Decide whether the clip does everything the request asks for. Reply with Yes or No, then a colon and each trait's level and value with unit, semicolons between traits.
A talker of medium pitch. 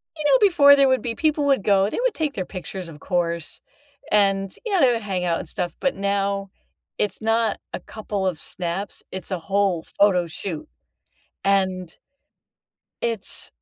No: high, 200 Hz